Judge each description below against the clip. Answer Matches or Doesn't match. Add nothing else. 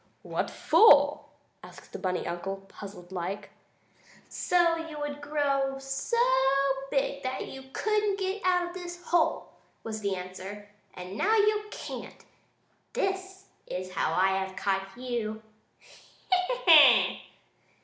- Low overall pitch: Doesn't match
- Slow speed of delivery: Matches